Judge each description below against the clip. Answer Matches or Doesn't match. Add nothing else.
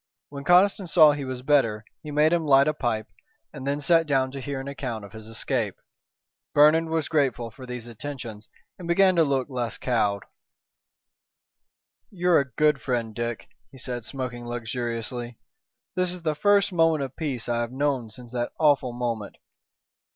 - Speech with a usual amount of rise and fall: Matches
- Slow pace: Doesn't match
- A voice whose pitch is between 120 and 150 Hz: Matches